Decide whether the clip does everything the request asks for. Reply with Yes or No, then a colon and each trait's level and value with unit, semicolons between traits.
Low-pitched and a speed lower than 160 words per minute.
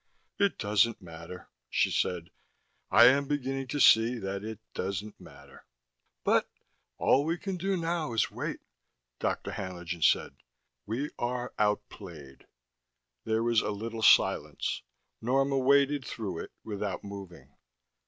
Yes: low, 110 Hz; slow, 135 wpm